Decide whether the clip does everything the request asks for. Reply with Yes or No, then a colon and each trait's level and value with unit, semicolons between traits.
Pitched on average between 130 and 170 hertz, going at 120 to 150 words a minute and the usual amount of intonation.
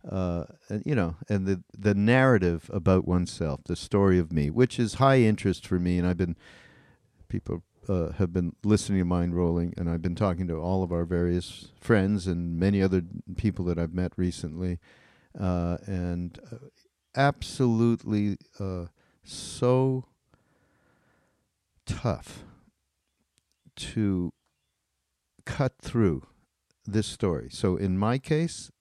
No: very low, 95 Hz; slow, 135 wpm; average, 3.7 semitones